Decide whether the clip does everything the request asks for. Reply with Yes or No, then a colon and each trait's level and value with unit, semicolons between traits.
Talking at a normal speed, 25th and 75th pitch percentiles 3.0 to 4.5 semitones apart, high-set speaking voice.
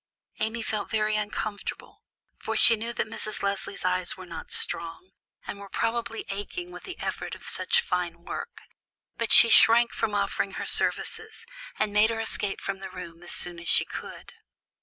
Yes: average, 180 wpm; average, 3.7 semitones; high, 210 Hz